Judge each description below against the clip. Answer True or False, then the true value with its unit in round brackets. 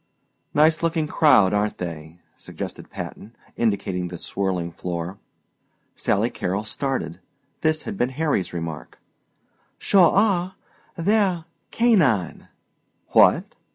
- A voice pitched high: False (115 Hz)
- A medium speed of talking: False (105 wpm)